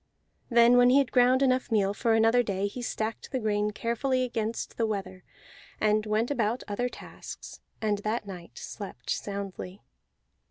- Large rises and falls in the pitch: No, average, 3.1 semitones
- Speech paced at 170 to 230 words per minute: No, average, 160 wpm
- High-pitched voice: Yes, high, 220 Hz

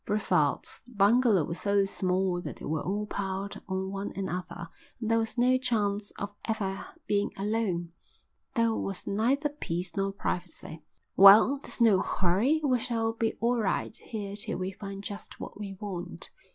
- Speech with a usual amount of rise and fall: Yes, average, 3.0 semitones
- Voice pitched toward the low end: No, high, 200 Hz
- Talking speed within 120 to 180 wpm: Yes, average, 165 wpm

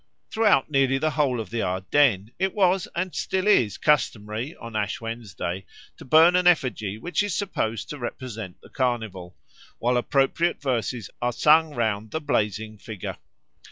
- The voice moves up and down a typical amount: No, wide, 6.3 semitones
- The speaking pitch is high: No, low, 125 Hz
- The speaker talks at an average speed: Yes, average, 160 wpm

